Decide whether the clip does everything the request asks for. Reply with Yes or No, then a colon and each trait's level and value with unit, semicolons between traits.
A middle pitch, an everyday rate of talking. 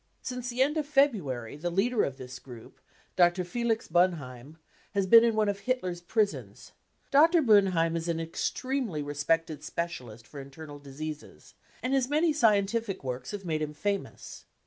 Yes: medium, 180 Hz; average, 160 wpm